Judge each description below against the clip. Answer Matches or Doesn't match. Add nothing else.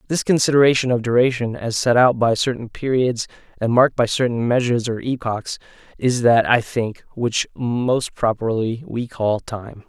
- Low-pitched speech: Matches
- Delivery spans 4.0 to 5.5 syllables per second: Matches